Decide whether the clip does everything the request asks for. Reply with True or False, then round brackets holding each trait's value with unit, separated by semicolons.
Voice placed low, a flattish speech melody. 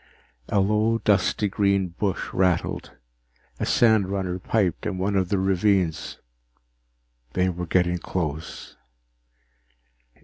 True (95 Hz; 2.2 semitones)